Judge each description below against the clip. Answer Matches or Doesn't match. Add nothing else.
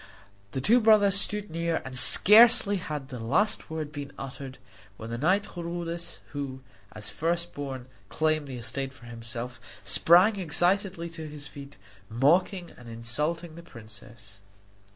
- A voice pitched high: Doesn't match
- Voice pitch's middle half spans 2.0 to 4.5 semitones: Doesn't match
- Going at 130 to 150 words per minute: Matches